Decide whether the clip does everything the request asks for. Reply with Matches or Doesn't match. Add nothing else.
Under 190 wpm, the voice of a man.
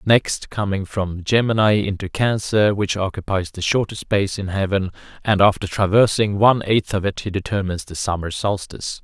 Matches